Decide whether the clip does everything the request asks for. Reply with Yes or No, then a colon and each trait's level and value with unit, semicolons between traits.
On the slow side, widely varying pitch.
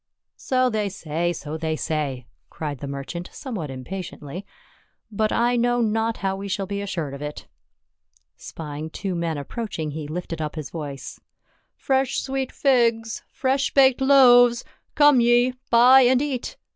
No: average, 160 wpm; wide, 7.7 semitones